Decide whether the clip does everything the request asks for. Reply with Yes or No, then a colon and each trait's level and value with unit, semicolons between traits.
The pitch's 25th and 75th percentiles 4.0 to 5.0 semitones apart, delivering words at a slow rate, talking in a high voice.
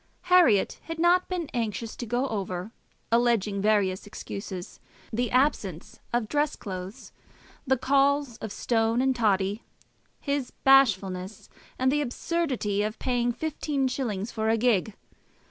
Yes: average, 4.7 semitones; slow, 130 wpm; high, 235 Hz